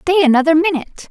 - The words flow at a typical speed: Yes, average, 165 wpm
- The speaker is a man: No, female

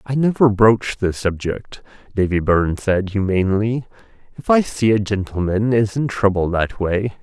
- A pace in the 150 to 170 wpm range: Yes, average, 160 wpm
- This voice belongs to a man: Yes, male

